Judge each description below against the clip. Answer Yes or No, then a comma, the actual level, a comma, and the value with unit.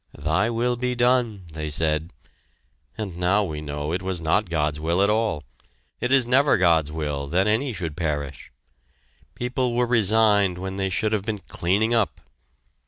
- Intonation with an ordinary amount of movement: No, wide, 6.1 semitones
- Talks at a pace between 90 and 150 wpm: No, average, 170 wpm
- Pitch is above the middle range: No, very low, 95 Hz